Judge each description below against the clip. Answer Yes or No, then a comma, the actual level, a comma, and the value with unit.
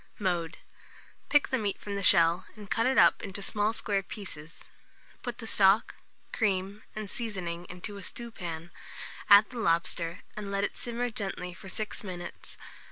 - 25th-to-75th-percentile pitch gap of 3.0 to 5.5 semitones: Yes, average, 3.3 semitones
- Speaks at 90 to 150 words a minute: No, average, 165 wpm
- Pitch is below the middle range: No, high, 200 Hz